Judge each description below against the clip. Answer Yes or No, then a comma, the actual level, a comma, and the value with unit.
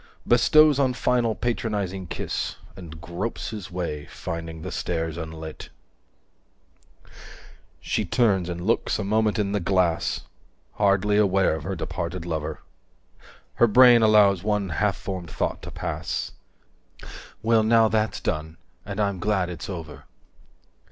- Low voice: Yes, very low, 95 Hz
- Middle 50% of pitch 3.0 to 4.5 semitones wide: Yes, average, 4.2 semitones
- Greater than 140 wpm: No, slow, 135 wpm